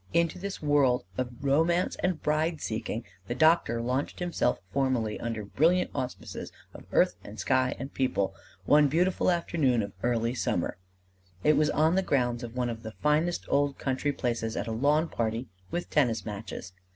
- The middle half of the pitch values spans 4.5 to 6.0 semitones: Yes, average, 5.2 semitones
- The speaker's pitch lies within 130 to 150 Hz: Yes, low, 135 Hz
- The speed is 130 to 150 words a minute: No, average, 170 wpm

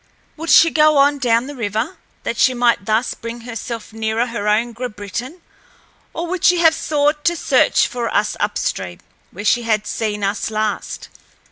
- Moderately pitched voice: No, high, 235 Hz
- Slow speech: No, average, 170 wpm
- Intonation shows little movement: No, average, 5.1 semitones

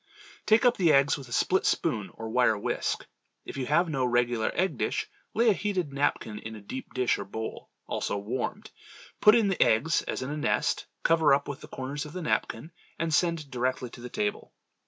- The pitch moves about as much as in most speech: No, wide, 5.7 semitones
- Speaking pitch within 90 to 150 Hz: Yes, medium, 140 Hz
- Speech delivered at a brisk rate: Yes, fast, 210 wpm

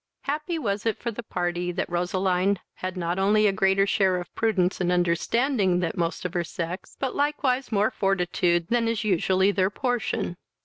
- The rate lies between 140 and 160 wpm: No, average, 180 wpm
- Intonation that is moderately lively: Yes, average, 4.0 semitones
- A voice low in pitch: No, high, 195 Hz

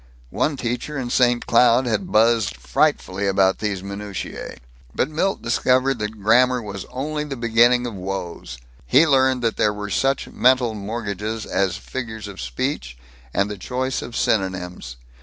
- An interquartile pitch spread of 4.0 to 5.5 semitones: Yes, average, 4.3 semitones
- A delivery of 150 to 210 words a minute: Yes, average, 155 wpm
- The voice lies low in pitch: Yes, low, 115 Hz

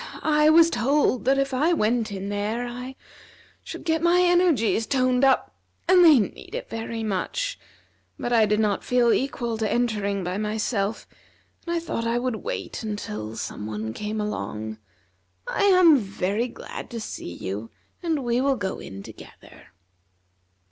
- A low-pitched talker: No, high, 235 Hz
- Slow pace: No, average, 160 wpm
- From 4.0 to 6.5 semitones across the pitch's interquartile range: Yes, average, 5.3 semitones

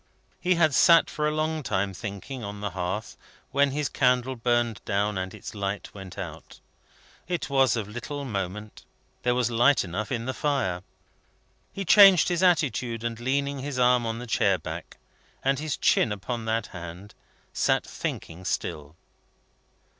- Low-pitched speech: Yes, low, 120 Hz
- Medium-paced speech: Yes, average, 160 wpm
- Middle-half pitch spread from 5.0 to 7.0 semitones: Yes, wide, 5.6 semitones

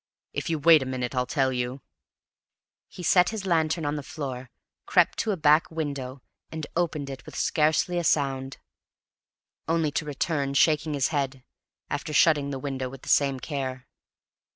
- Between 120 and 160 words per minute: No, average, 170 wpm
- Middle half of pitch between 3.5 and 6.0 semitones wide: No, average, 3.1 semitones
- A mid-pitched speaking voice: Yes, medium, 145 Hz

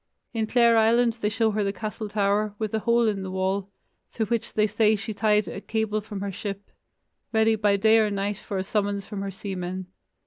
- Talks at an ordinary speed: No, fast, 210 wpm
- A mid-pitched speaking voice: No, high, 210 Hz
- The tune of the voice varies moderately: No, narrow, 1.8 semitones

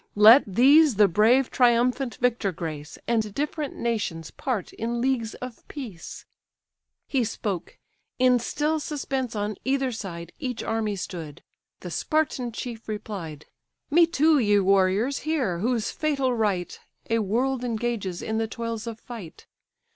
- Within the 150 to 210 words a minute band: No, average, 140 wpm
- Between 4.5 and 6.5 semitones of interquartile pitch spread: No, average, 4.1 semitones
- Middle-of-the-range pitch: No, high, 230 Hz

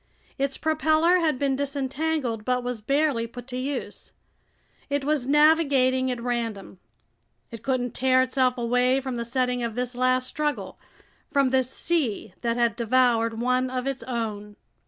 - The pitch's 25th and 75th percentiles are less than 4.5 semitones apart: Yes, narrow, 2.5 semitones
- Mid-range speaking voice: No, very high, 255 Hz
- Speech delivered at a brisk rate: No, average, 155 wpm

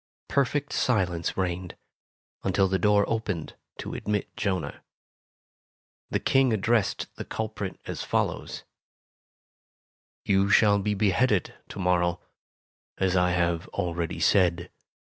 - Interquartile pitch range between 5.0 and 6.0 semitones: No, average, 3.2 semitones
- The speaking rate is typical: No, slow, 110 wpm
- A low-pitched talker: Yes, very low, 95 Hz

